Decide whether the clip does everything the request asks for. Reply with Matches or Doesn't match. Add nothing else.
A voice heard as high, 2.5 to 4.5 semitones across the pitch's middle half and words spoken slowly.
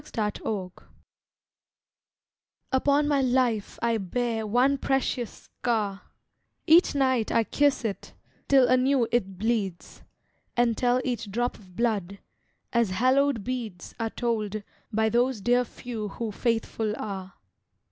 Matches